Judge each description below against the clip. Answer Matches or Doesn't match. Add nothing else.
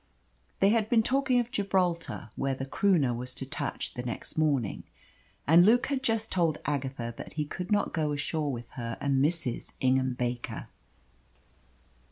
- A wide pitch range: Matches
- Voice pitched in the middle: Matches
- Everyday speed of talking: Matches